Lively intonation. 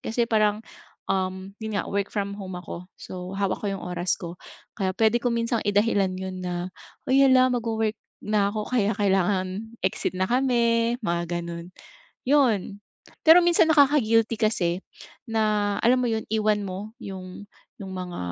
No: average, 3.6 semitones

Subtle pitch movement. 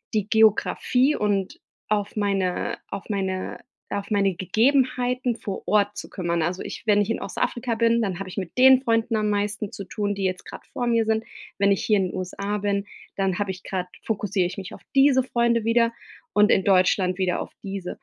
No: average, 3.0 semitones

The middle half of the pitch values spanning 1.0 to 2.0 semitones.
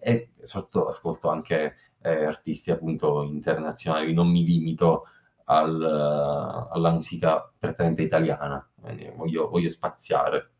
Yes: narrow, 1.5 semitones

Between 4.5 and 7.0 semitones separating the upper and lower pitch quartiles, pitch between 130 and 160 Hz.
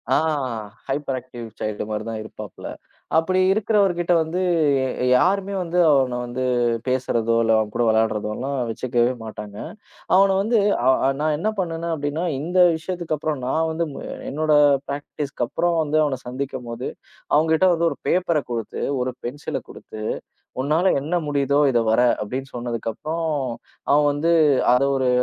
Yes: average, 5.2 semitones; medium, 140 Hz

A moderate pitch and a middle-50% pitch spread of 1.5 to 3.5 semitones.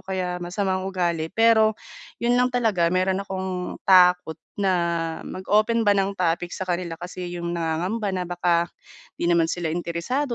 Yes: medium, 180 Hz; narrow, 2.5 semitones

